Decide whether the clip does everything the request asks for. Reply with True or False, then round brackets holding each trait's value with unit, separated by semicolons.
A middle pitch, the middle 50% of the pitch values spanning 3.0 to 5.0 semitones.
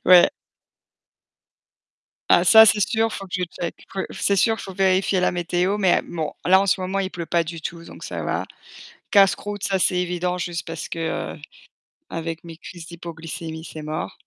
False (180 Hz; 2.5 semitones)